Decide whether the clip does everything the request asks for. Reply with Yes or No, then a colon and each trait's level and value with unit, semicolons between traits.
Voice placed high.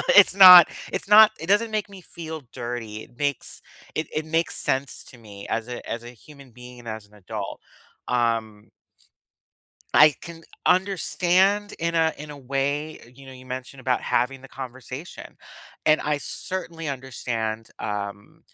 No: low, 135 Hz